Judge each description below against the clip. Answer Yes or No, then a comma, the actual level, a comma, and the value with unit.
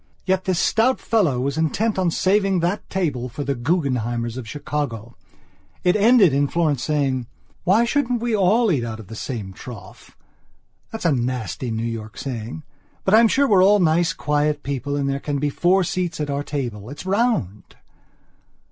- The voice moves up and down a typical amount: No, wide, 7.2 semitones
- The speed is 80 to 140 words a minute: No, average, 175 wpm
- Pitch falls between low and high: Yes, medium, 150 Hz